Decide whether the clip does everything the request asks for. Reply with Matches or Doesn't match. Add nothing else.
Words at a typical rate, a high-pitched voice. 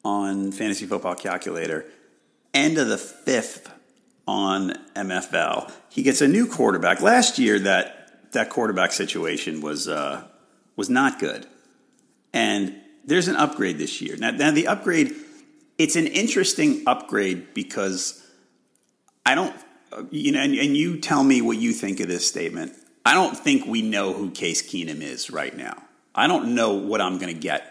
Matches